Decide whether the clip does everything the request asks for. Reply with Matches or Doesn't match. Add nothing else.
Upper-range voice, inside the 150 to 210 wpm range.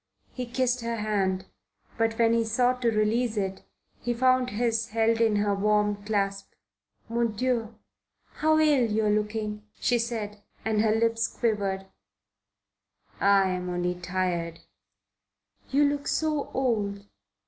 Doesn't match